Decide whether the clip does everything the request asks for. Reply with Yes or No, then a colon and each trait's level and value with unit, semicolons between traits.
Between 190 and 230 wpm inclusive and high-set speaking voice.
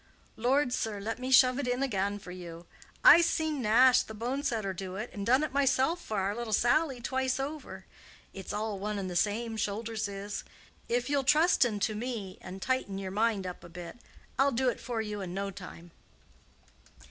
Yes: average, 195 wpm; high, 225 Hz